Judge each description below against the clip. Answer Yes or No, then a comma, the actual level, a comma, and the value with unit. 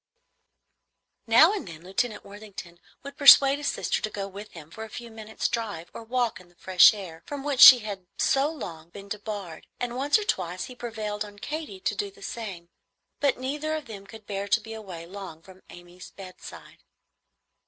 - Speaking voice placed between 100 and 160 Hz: No, high, 210 Hz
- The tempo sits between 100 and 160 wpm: No, average, 195 wpm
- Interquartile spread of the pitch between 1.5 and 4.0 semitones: No, average, 4.7 semitones